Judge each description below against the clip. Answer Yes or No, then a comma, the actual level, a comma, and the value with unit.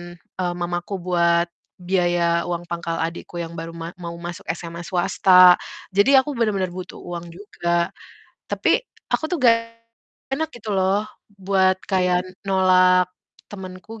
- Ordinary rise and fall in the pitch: No, narrow, 2.0 semitones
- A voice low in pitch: No, medium, 180 Hz